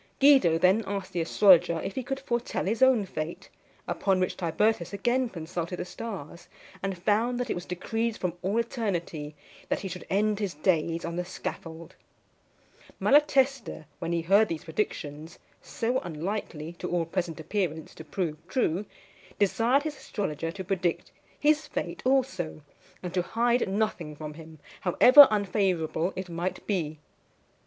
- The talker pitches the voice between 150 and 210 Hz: Yes, medium, 185 Hz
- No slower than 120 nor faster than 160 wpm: Yes, average, 155 wpm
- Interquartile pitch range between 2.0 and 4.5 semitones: No, average, 5.1 semitones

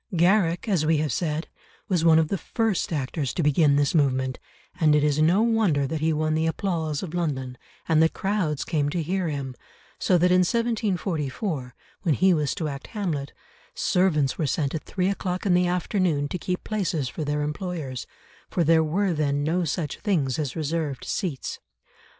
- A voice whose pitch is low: No, medium, 160 Hz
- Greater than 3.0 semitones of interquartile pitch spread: Yes, average, 3.7 semitones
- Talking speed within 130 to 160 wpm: No, average, 185 wpm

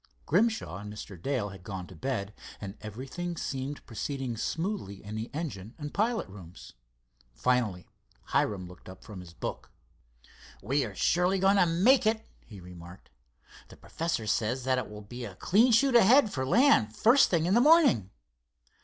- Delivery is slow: No, average, 165 wpm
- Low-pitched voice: Yes, low, 130 Hz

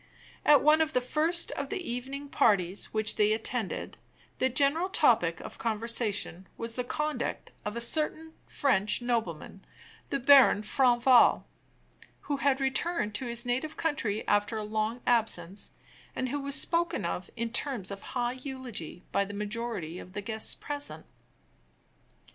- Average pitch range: Yes, average, 4.9 semitones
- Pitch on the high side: Yes, high, 240 Hz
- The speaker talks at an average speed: Yes, average, 150 wpm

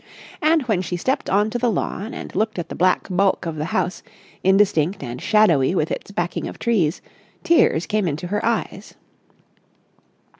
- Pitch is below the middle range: No, high, 190 Hz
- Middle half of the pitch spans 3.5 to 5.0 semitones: Yes, average, 4.3 semitones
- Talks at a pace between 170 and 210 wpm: Yes, average, 175 wpm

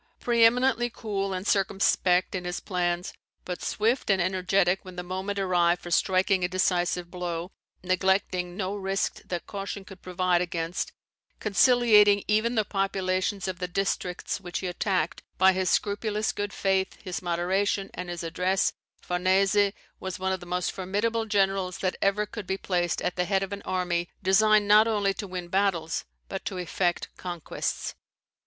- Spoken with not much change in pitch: Yes, narrow, 2.0 semitones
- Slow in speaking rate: No, average, 165 wpm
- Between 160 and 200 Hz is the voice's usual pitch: Yes, high, 190 Hz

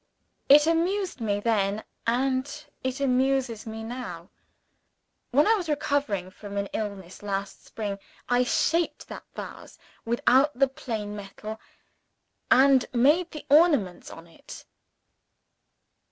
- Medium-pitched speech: No, high, 245 Hz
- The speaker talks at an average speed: No, slow, 125 wpm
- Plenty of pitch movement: Yes, wide, 5.7 semitones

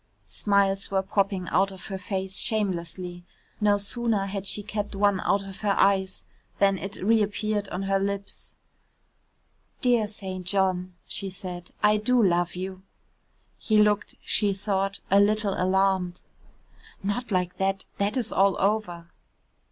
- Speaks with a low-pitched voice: No, high, 195 Hz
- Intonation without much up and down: Yes, narrow, 1.6 semitones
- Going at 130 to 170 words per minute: Yes, average, 145 wpm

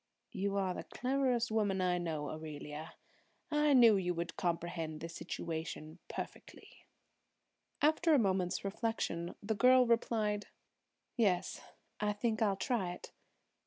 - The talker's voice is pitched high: Yes, high, 195 Hz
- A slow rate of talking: Yes, slow, 125 wpm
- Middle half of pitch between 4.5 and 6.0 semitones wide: Yes, average, 5.2 semitones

